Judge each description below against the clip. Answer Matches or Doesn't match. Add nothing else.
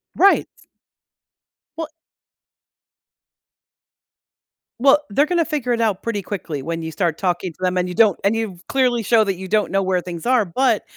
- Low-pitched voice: Doesn't match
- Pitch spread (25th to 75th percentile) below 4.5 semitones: Doesn't match